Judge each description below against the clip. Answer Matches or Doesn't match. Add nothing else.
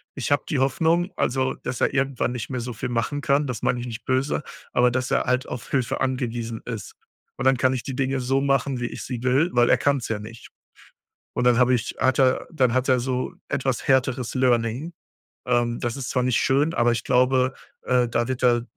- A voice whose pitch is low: Matches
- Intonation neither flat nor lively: Doesn't match